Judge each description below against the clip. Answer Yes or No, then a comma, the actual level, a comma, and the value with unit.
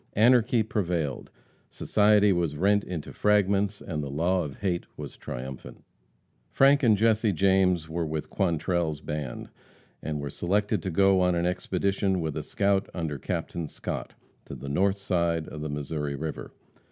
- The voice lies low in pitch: Yes, very low, 90 Hz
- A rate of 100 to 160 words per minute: Yes, average, 155 wpm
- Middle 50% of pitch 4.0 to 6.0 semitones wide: Yes, average, 4.5 semitones